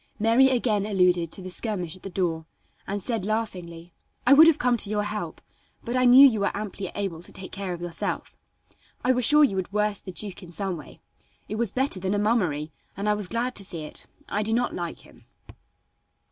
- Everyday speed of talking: No, fast, 220 wpm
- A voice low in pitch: No, high, 205 Hz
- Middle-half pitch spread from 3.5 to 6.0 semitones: Yes, average, 4.1 semitones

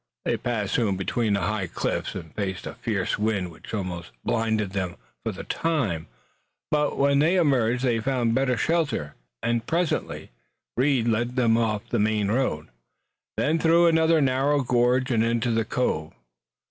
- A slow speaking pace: No, average, 160 wpm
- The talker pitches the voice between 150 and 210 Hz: No, low, 120 Hz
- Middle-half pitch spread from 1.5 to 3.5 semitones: No, average, 4.5 semitones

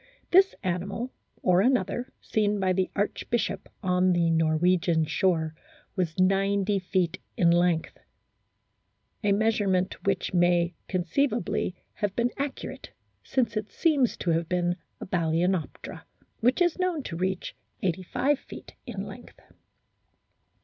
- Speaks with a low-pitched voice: No, medium, 185 Hz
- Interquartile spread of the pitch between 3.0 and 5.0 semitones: Yes, average, 3.8 semitones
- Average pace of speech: No, slow, 125 wpm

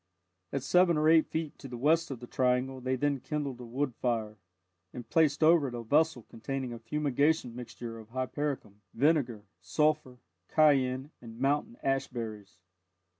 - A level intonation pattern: No, average, 3.9 semitones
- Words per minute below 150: No, average, 165 wpm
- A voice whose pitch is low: Yes, low, 130 Hz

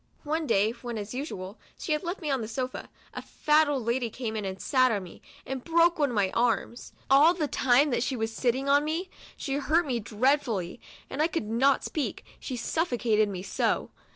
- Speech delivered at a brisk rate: Yes, fast, 210 wpm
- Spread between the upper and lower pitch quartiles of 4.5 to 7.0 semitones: Yes, average, 5.0 semitones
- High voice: Yes, very high, 255 Hz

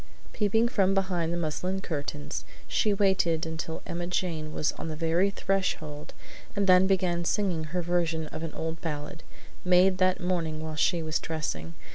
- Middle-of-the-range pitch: Yes, medium, 170 Hz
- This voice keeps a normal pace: Yes, average, 165 wpm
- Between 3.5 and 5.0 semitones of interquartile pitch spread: No, average, 2.9 semitones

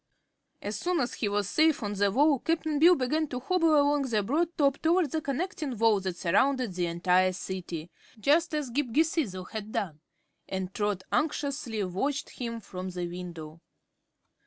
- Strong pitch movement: Yes, wide, 7.9 semitones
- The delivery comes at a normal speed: Yes, average, 170 wpm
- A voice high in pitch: Yes, high, 235 Hz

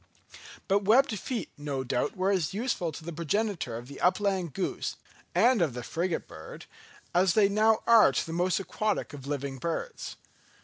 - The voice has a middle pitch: Yes, medium, 180 Hz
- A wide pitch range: Yes, wide, 6.2 semitones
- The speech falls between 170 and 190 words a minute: Yes, average, 175 wpm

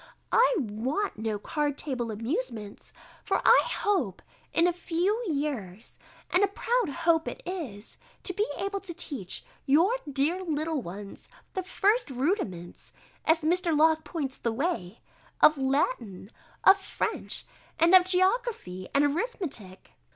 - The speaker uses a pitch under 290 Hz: No, very high, 310 Hz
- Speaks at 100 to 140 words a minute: Yes, slow, 135 wpm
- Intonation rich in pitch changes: Yes, wide, 8.0 semitones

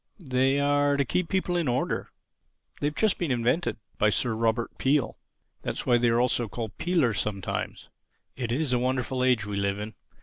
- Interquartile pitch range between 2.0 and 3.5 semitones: No, average, 3.9 semitones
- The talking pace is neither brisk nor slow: Yes, average, 175 wpm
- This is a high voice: No, low, 125 Hz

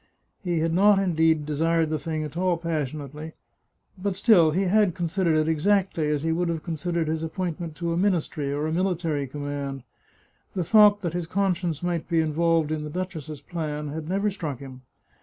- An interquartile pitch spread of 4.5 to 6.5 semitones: No, average, 2.7 semitones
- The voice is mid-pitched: Yes, medium, 165 Hz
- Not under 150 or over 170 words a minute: No, average, 190 wpm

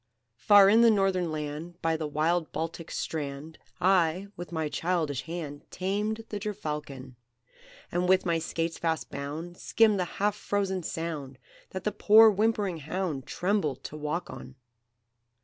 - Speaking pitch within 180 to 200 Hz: No, medium, 170 Hz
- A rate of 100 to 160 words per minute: Yes, average, 150 wpm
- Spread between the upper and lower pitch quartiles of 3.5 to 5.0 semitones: Yes, average, 4.0 semitones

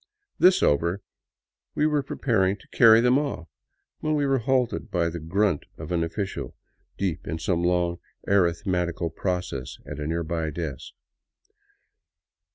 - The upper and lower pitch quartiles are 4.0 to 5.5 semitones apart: Yes, average, 5.2 semitones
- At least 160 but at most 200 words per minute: No, average, 140 wpm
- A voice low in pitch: Yes, very low, 90 Hz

